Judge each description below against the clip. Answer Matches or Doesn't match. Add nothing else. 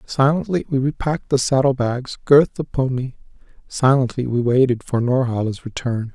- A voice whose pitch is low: Matches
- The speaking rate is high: Doesn't match